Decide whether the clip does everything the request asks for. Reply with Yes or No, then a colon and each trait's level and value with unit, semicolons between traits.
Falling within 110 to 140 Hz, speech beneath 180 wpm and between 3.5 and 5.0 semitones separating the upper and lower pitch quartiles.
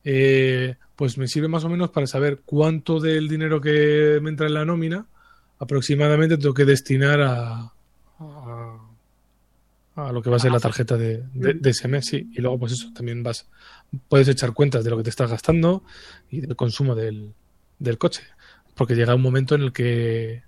No: low, 135 Hz; average, 185 wpm; average, 4.0 semitones